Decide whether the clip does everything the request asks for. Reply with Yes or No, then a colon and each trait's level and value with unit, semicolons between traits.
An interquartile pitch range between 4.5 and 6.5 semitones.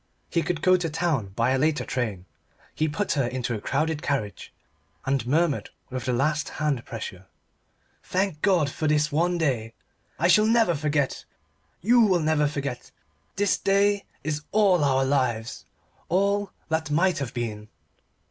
Yes: average, 5.3 semitones